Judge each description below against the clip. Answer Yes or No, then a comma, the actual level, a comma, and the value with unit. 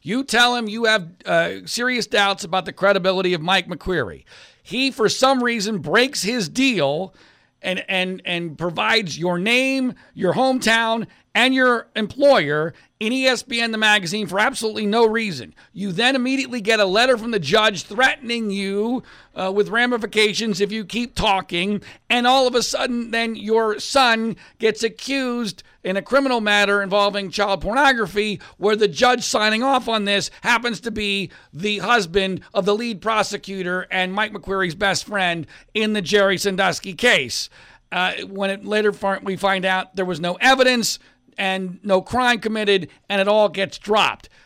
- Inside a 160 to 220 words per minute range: Yes, average, 165 wpm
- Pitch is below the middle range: No, high, 210 Hz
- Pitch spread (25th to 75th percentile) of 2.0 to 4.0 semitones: Yes, average, 3.4 semitones